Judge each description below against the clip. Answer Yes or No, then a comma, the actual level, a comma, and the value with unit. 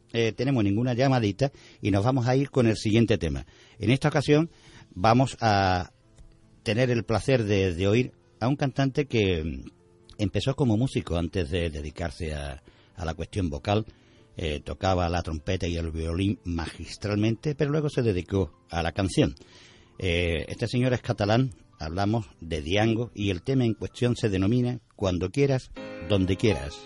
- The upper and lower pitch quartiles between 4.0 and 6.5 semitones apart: Yes, wide, 5.6 semitones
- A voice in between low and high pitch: No, low, 105 Hz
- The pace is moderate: Yes, average, 165 wpm